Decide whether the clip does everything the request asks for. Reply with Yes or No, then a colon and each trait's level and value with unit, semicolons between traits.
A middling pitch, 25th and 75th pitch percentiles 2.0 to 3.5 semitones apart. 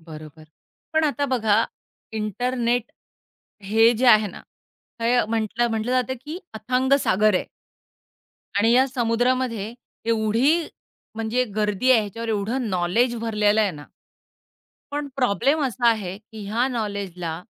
No: high, 225 Hz; average, 3.2 semitones